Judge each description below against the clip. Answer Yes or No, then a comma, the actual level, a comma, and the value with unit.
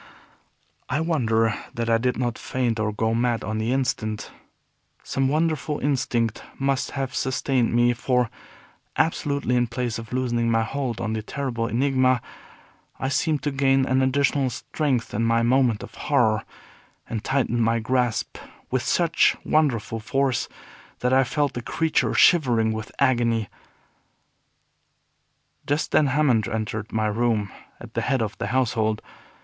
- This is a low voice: Yes, low, 125 Hz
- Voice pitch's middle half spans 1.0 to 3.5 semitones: Yes, average, 3.1 semitones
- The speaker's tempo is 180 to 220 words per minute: No, average, 145 wpm